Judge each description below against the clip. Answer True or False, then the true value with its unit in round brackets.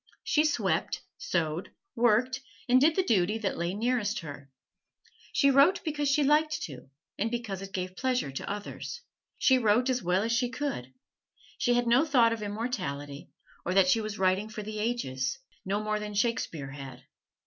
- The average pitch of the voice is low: False (215 Hz)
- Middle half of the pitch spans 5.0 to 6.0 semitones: True (5.5 semitones)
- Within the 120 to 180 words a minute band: True (175 wpm)